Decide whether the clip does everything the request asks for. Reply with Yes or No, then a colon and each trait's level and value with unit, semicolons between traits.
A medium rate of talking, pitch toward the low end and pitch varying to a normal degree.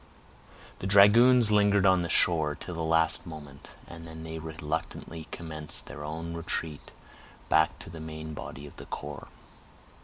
No: average, 155 wpm; very low, 80 Hz; narrow, 2.0 semitones